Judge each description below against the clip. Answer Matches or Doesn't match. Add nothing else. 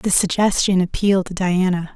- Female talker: Matches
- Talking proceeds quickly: Doesn't match